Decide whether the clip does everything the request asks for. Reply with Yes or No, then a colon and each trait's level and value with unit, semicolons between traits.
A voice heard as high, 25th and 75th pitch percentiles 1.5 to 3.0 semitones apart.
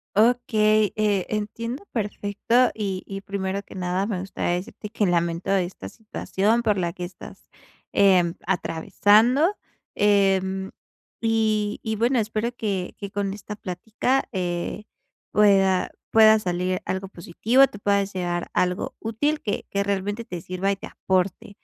Yes: high, 200 Hz; average, 2.7 semitones